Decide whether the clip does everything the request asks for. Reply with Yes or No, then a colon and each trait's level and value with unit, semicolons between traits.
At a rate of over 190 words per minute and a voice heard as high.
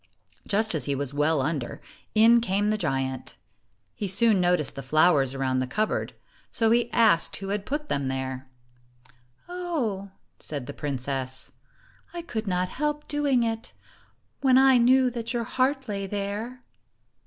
No: average, 155 wpm; high, 200 Hz